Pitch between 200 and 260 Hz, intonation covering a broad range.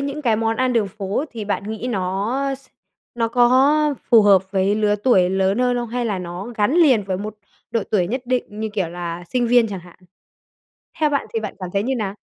No: high, 220 Hz; average, 4.3 semitones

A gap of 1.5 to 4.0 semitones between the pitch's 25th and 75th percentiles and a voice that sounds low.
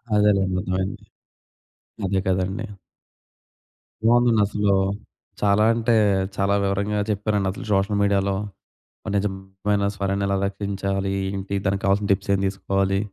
No: narrow, 1.0 semitones; low, 100 Hz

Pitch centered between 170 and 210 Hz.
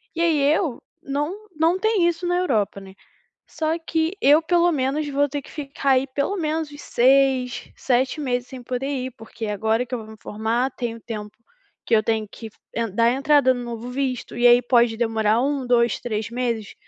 No: very high, 255 Hz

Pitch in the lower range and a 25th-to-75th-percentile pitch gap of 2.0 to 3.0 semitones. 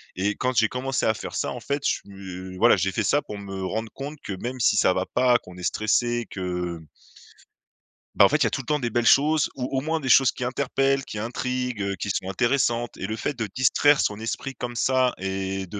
No: low, 120 Hz; average, 5.1 semitones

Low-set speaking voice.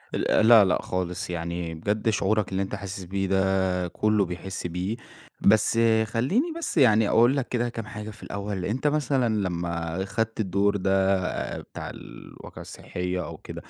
Yes: low, 100 Hz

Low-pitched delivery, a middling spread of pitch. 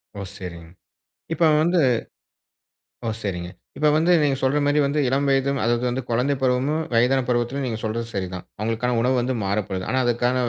Yes: low, 125 Hz; average, 3.5 semitones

